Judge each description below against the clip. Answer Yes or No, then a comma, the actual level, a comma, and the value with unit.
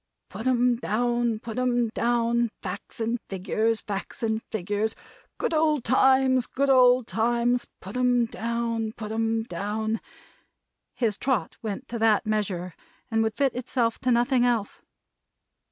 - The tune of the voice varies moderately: No, narrow, 2.0 semitones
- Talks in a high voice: Yes, high, 230 Hz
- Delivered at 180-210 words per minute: No, average, 140 wpm